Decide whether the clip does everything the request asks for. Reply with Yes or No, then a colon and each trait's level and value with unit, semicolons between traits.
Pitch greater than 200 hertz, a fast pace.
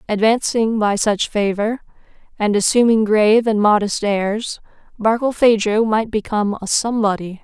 No: high, 215 Hz; slow, 120 wpm